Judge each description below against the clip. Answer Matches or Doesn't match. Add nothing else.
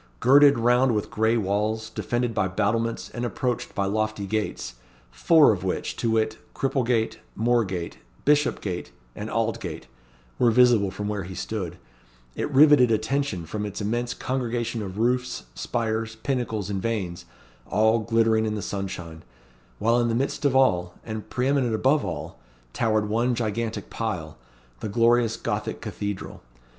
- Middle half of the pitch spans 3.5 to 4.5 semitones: Doesn't match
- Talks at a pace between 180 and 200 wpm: Doesn't match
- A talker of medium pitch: Doesn't match